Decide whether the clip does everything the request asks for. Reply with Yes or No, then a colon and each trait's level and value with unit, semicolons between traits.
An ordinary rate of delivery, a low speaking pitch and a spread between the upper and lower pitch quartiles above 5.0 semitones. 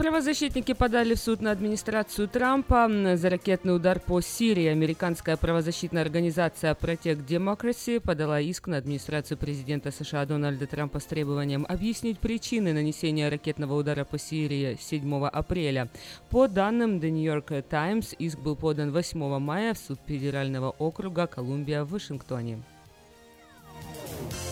No: average, 130 wpm; medium, 160 Hz; wide, 5.4 semitones